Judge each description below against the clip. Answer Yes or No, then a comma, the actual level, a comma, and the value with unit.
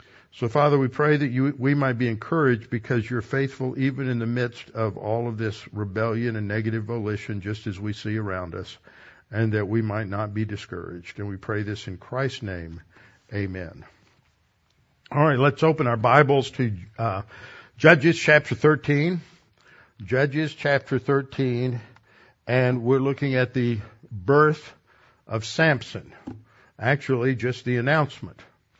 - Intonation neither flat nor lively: Yes, average, 4.3 semitones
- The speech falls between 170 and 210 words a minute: No, average, 150 wpm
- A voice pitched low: Yes, low, 120 Hz